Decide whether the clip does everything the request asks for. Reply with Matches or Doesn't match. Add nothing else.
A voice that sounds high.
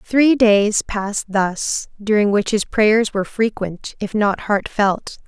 Matches